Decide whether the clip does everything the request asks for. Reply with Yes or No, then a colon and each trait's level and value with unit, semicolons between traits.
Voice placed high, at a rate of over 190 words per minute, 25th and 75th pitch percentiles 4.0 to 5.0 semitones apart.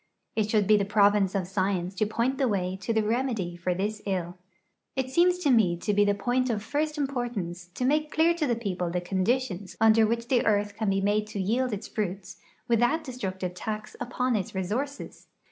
Yes: high, 215 Hz; fast, 205 wpm; average, 4.5 semitones